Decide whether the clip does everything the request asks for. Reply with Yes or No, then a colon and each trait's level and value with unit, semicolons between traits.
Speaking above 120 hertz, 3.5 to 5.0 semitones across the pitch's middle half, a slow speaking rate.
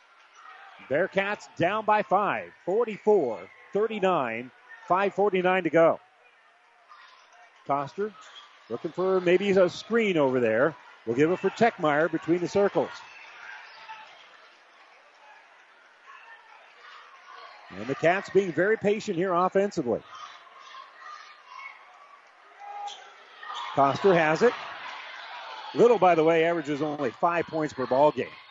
Yes: high, 190 Hz; average, 4.7 semitones; slow, 100 wpm